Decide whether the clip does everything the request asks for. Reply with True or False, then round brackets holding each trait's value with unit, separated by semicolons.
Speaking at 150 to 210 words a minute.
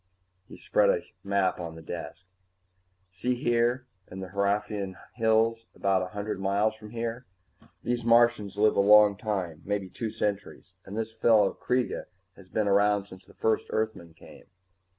True (160 wpm)